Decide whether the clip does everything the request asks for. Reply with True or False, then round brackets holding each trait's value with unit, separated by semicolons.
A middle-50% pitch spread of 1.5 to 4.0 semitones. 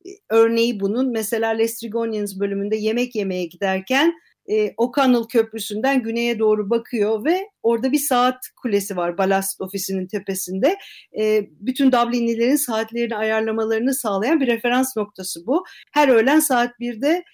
True (3.4 semitones)